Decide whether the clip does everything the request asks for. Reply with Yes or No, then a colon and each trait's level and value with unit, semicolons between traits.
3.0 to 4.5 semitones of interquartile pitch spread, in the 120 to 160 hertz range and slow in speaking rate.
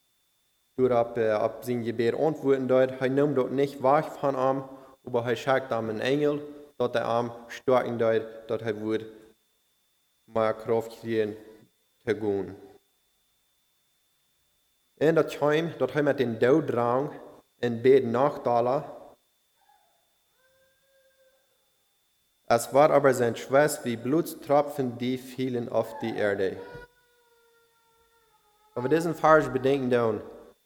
Yes: average, 4.2 semitones; low, 130 Hz; slow, 120 wpm